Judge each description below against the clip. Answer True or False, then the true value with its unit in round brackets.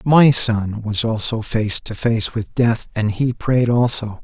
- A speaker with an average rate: True (185 wpm)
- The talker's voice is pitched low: True (115 Hz)